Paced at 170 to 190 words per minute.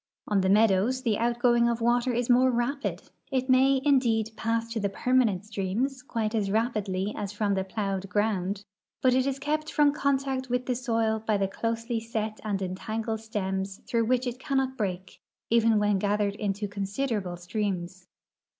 Yes: average, 175 wpm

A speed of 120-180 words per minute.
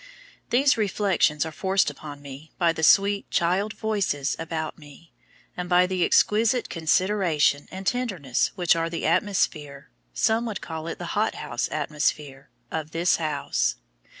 Yes: average, 145 wpm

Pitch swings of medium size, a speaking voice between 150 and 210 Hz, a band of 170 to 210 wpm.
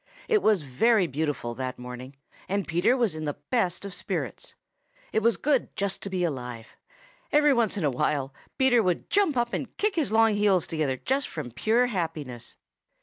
No: wide, 8.8 semitones; high, 190 Hz; average, 185 wpm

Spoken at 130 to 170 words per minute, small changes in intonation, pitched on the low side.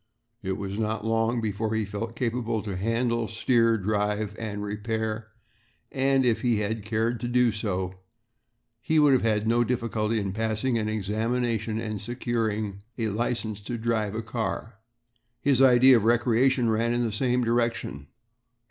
Yes: average, 155 wpm; narrow, 2.0 semitones; low, 115 Hz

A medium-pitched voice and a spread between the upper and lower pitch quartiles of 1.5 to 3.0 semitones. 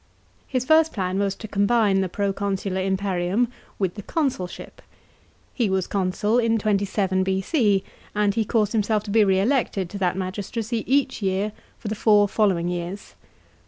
No: high, 200 Hz; narrow, 2.5 semitones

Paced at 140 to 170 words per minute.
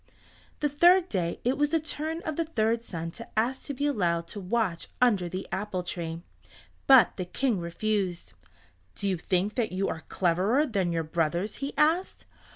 No: average, 180 wpm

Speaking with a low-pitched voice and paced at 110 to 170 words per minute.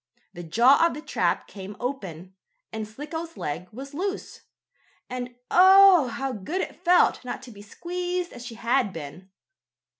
No: very high, 255 Hz; average, 155 wpm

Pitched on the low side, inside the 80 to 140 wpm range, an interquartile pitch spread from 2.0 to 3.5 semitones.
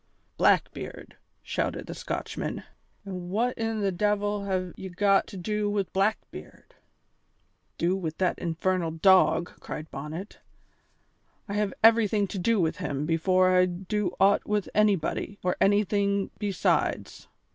No: high, 195 Hz; slow, 135 wpm; narrow, 2.5 semitones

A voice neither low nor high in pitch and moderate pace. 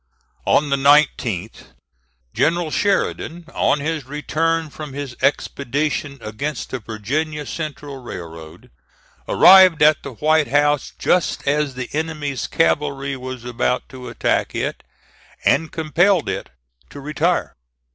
No: medium, 145 Hz; slow, 120 wpm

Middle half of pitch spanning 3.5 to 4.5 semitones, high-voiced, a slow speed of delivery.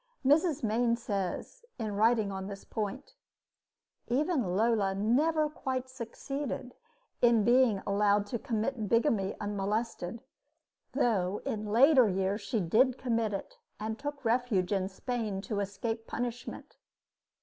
Yes: average, 3.8 semitones; high, 225 Hz; slow, 125 wpm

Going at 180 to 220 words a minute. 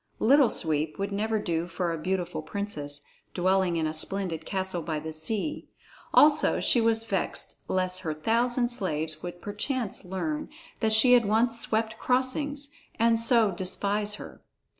No: average, 155 wpm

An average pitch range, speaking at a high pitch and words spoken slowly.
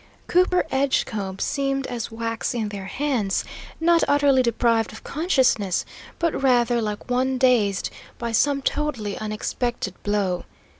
Yes: average, 4.4 semitones; high, 240 Hz; slow, 130 wpm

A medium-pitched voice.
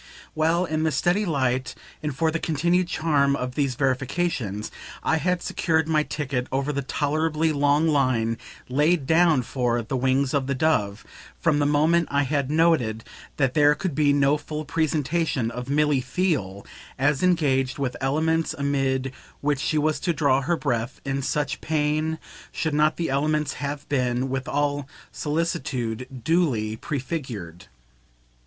Yes: medium, 145 Hz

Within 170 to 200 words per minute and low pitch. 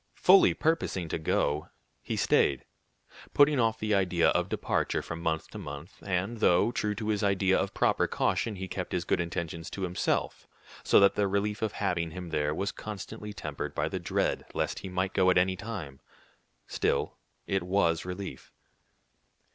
Yes: average, 175 wpm; very low, 95 Hz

